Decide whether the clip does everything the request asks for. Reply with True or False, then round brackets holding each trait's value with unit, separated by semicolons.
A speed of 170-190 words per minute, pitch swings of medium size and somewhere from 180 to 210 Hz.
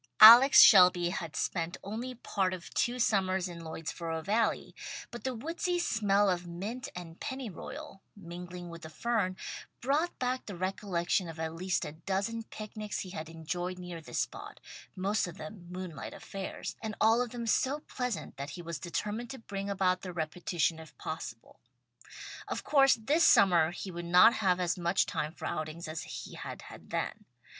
True (175 wpm; 4.6 semitones; 185 Hz)